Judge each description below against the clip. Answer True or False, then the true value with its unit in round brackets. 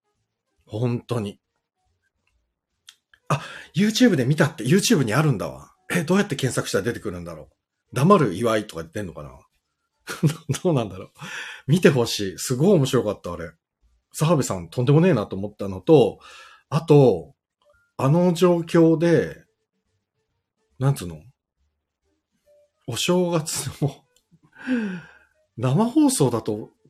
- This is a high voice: False (135 Hz)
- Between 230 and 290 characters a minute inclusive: True (270 characters per minute)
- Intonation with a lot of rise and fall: True (8.5 semitones)